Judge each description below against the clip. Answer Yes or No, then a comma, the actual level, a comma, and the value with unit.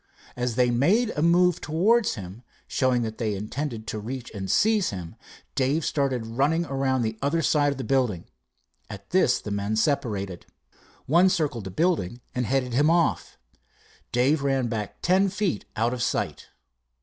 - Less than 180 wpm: Yes, average, 165 wpm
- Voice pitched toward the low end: Yes, low, 130 Hz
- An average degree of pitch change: No, wide, 6.1 semitones